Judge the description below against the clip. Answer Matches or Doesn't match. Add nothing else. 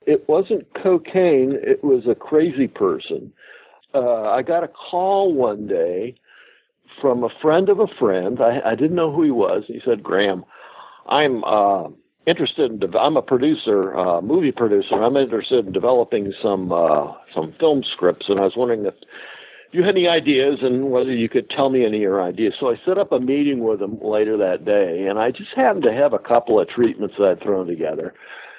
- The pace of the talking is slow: Doesn't match